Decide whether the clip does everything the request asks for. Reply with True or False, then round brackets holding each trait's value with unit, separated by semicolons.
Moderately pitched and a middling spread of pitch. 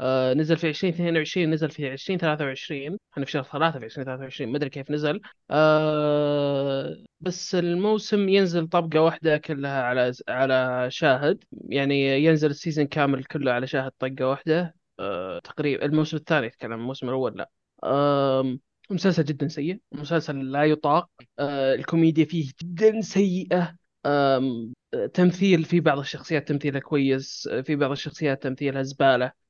True (150 Hz; 3.3 semitones)